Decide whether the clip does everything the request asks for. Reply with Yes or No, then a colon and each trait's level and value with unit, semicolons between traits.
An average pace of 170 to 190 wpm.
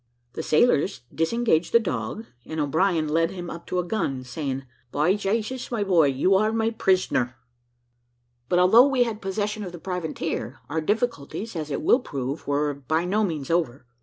Yes: average, 175 wpm